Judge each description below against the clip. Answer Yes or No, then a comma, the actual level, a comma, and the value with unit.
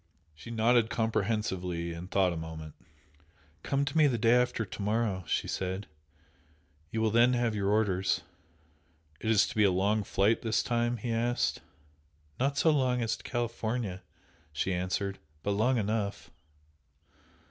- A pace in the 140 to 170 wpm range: Yes, average, 155 wpm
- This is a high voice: No, low, 110 Hz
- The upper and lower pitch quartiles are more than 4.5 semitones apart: No, average, 3.7 semitones